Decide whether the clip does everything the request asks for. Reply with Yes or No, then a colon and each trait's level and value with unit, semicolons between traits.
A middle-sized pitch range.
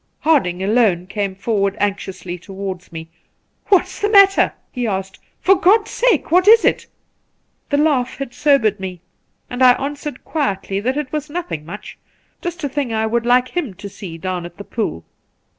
No: wide, 7.6 semitones